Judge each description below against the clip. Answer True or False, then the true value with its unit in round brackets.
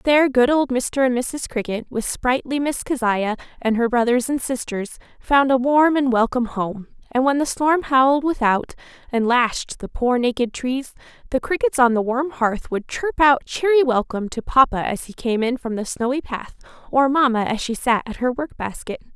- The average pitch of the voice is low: False (255 Hz)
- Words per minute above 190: True (200 wpm)